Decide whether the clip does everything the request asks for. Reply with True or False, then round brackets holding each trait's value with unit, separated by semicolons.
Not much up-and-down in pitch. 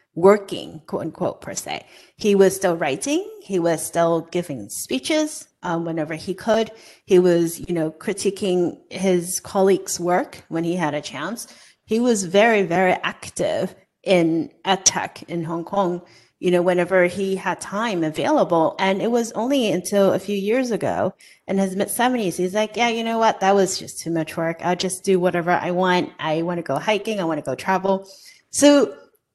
False (3.0 semitones)